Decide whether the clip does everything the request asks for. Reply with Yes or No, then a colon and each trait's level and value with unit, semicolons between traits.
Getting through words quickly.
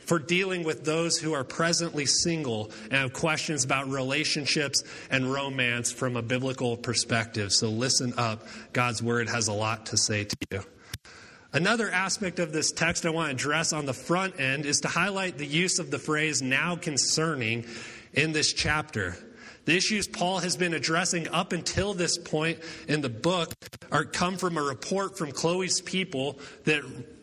No: average, 175 wpm